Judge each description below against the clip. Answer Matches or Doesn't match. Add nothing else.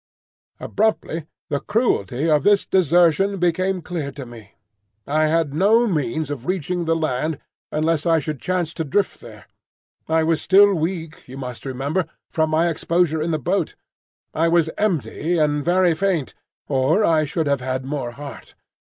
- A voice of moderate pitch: Matches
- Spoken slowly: Doesn't match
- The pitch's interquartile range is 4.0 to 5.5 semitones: Doesn't match